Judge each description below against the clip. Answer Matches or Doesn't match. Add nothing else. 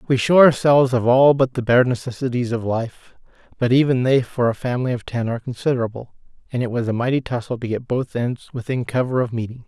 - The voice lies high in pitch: Doesn't match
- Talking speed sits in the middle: Doesn't match